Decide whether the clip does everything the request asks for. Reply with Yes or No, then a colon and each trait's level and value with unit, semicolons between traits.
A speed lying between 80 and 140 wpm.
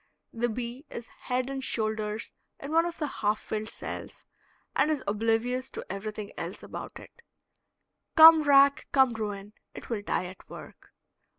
No: average, 160 wpm